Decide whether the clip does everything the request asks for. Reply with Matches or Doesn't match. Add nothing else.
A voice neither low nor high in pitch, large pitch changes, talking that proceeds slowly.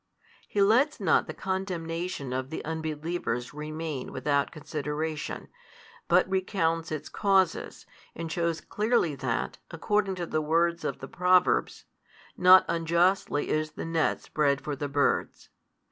Doesn't match